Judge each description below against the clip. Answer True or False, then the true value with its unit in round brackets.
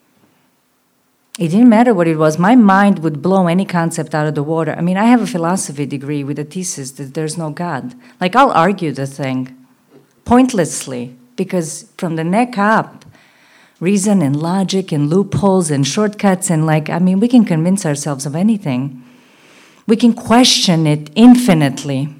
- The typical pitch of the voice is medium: True (170 Hz)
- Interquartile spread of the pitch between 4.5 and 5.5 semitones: True (5.1 semitones)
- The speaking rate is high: False (170 wpm)